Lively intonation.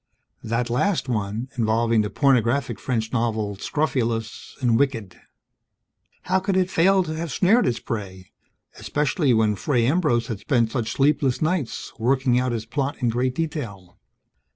No: average, 4.7 semitones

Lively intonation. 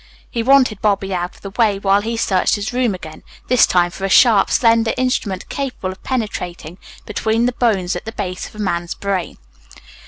No: average, 3.7 semitones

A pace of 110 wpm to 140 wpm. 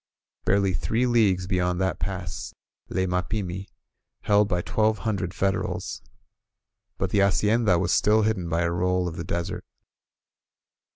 Yes: slow, 135 wpm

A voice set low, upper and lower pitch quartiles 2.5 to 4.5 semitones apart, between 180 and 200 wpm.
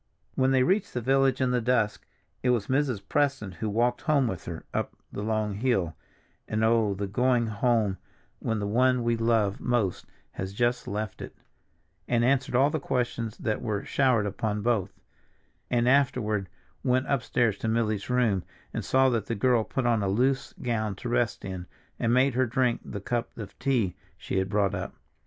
Yes: low, 115 Hz; average, 3.5 semitones; average, 185 wpm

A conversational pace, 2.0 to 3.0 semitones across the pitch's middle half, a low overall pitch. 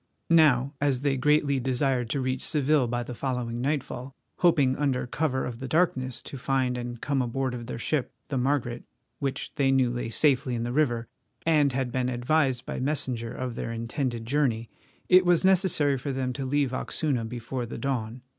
Yes: average, 185 wpm; average, 2.7 semitones; low, 130 Hz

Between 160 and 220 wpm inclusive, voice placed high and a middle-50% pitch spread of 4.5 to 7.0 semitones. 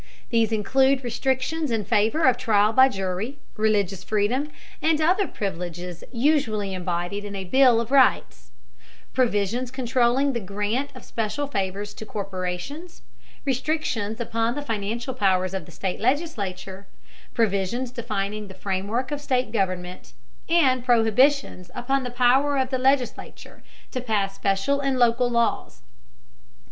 No: slow, 135 wpm; high, 230 Hz; average, 4.8 semitones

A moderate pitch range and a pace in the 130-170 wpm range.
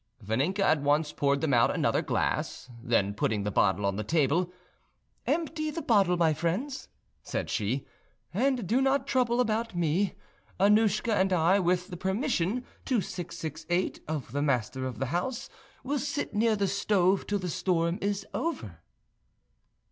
No: wide, 7.1 semitones; average, 155 wpm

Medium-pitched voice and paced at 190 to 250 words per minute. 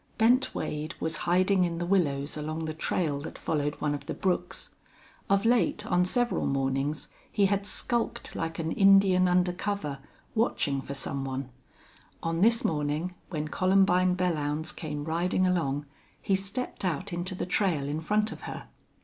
No: medium, 175 Hz; average, 165 wpm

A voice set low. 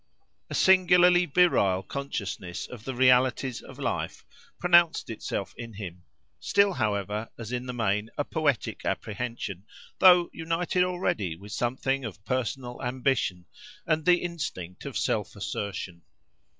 Yes: low, 125 Hz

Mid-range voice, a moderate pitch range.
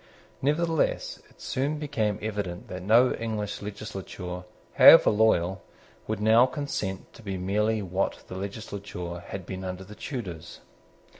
No: low, 105 Hz; average, 3.2 semitones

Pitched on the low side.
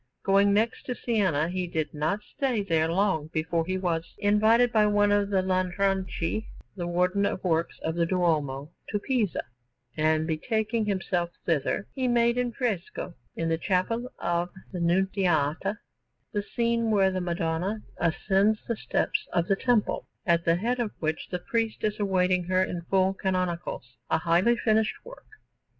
No: high, 190 Hz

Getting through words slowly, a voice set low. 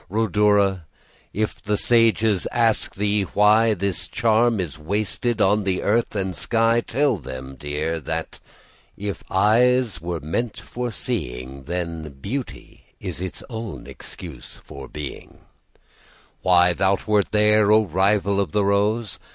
Yes: slow, 120 wpm; low, 100 Hz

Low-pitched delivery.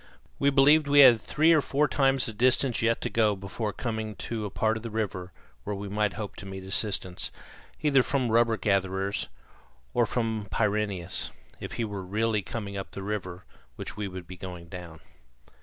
Yes: low, 105 Hz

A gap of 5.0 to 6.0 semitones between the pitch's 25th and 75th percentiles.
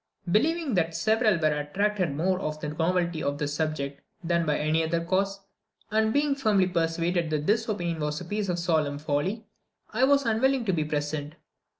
Yes: wide, 5.5 semitones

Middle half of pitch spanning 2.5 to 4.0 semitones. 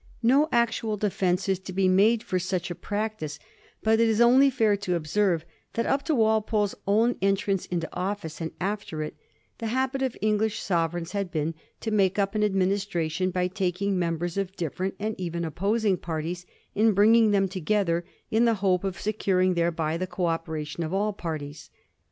Yes: average, 3.7 semitones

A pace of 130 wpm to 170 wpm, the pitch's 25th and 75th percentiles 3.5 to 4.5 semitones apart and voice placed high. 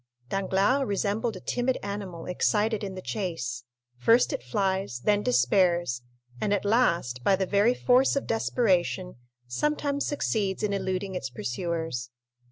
Yes: average, 140 wpm; average, 4.1 semitones; high, 195 Hz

